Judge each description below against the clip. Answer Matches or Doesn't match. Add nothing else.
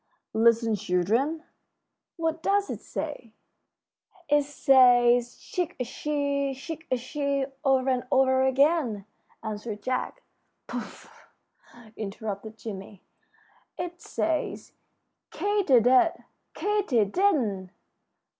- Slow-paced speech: Matches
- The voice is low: Doesn't match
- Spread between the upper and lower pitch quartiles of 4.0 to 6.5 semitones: Matches